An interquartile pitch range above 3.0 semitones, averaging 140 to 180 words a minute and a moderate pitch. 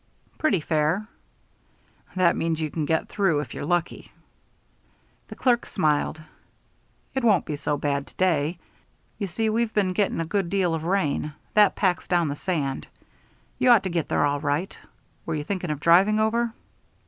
Yes: average, 4.7 semitones; average, 170 wpm; medium, 175 Hz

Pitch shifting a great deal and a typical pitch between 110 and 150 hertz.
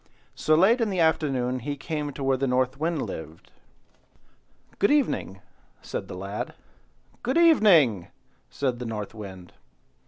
Yes: wide, 6.9 semitones; low, 135 Hz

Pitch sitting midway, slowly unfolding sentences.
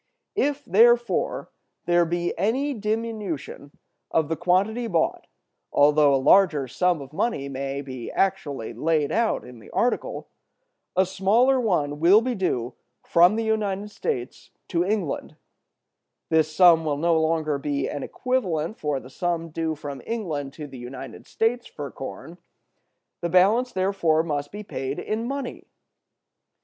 No: medium, 170 Hz; average, 145 wpm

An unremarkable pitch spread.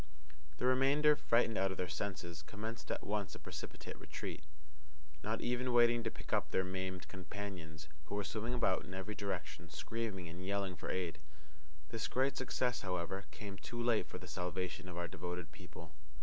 Yes: average, 4.4 semitones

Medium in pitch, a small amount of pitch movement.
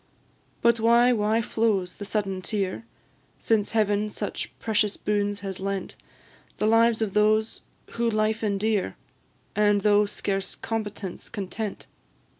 No: high, 210 Hz; narrow, 1.8 semitones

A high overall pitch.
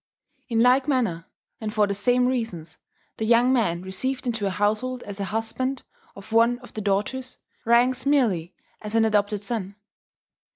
Yes: high, 225 Hz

